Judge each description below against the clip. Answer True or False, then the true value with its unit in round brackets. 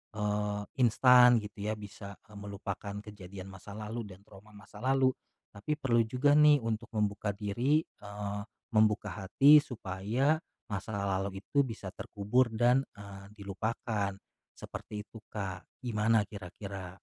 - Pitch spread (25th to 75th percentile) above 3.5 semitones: False (3.0 semitones)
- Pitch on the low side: True (105 Hz)